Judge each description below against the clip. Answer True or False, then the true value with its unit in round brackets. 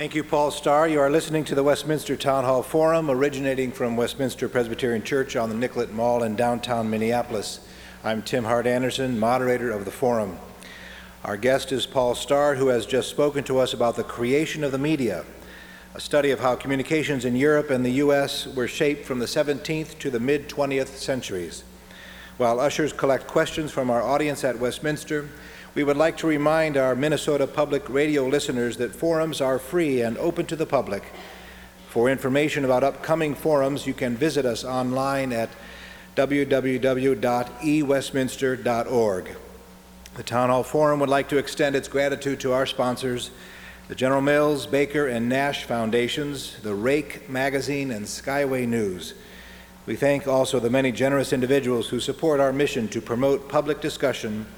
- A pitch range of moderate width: True (3.2 semitones)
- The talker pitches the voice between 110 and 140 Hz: True (135 Hz)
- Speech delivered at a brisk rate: False (165 wpm)